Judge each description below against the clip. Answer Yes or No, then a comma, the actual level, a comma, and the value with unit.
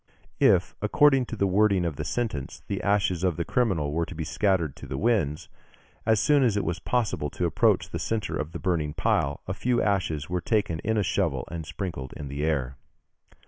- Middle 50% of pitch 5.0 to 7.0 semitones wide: Yes, wide, 5.5 semitones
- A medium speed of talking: No, fast, 210 wpm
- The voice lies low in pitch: Yes, very low, 90 Hz